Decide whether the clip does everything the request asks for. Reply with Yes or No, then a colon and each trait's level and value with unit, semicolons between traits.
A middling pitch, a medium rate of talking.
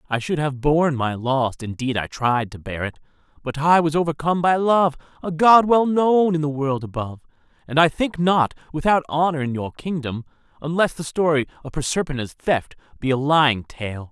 Yes: medium, 150 Hz; average, 190 wpm